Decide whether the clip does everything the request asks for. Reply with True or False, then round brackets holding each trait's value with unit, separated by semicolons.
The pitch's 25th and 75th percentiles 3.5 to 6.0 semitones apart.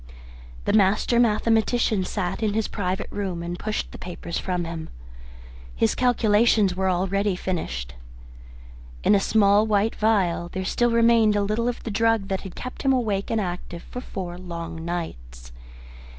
True (3.9 semitones)